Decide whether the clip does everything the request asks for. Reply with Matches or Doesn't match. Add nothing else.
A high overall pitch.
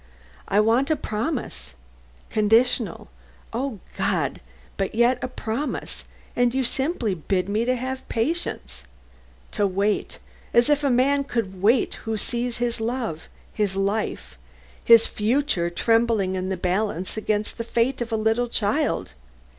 Matches